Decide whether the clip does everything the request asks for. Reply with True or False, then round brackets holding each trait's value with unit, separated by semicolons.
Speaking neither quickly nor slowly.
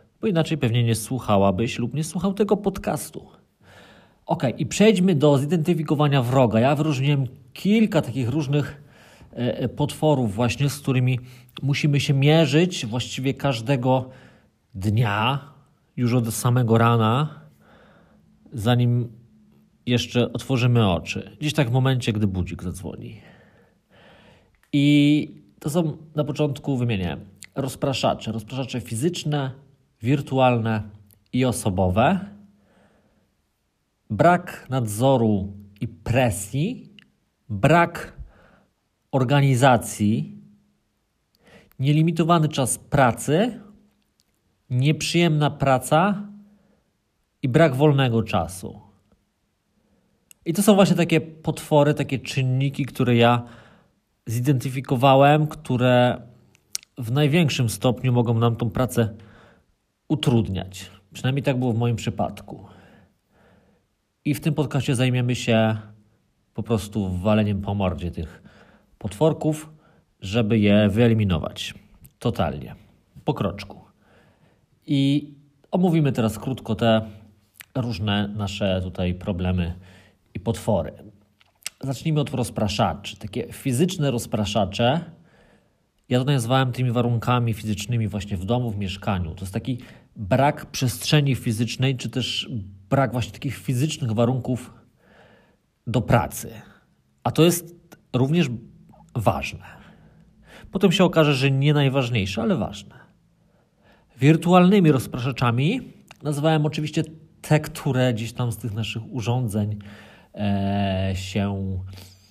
False (100 wpm)